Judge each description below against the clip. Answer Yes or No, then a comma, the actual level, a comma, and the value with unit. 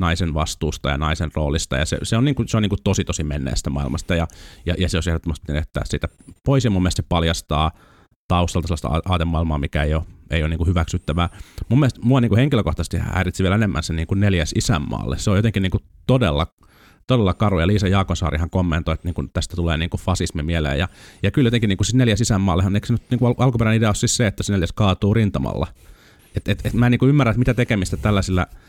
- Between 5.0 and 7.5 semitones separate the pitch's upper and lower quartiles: No, average, 4.4 semitones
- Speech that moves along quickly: Yes, fast, 220 wpm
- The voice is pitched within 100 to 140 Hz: No, very low, 90 Hz